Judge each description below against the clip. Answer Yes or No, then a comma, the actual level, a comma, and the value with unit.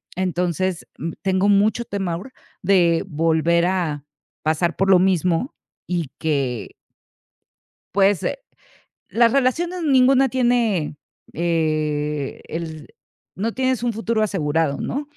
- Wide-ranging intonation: Yes, wide, 6.1 semitones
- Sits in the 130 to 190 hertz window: Yes, medium, 185 Hz